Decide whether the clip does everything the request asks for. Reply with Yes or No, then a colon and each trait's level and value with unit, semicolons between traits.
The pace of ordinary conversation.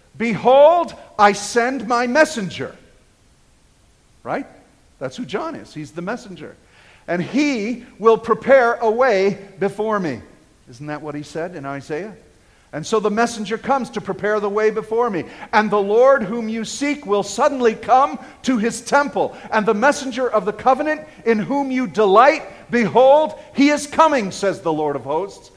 Yes: average, 165 wpm